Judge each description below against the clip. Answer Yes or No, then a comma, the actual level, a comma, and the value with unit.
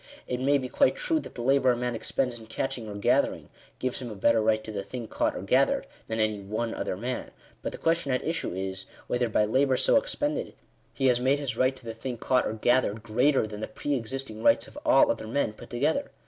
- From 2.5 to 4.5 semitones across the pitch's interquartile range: Yes, average, 3.6 semitones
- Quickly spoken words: Yes, fast, 240 wpm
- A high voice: No, low, 125 Hz